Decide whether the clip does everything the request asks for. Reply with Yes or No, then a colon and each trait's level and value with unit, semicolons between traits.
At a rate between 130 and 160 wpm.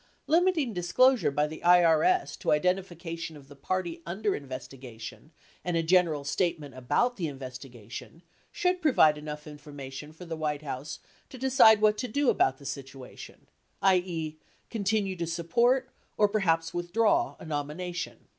Yes: average, 150 wpm